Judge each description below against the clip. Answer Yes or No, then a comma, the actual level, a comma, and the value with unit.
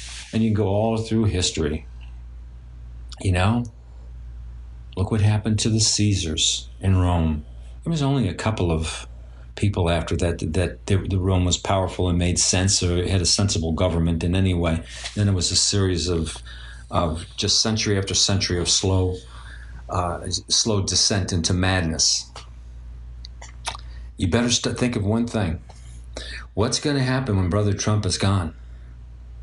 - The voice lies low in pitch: Yes, very low, 90 Hz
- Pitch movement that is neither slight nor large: No, wide, 8.7 semitones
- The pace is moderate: Yes, average, 160 wpm